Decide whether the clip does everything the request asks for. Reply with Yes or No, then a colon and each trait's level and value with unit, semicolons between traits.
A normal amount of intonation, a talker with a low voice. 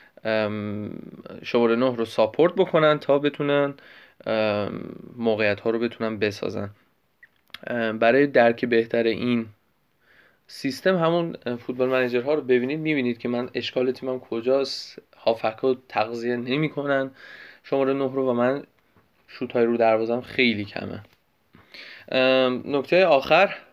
Yes: average, 3.1 semitones; low, 125 Hz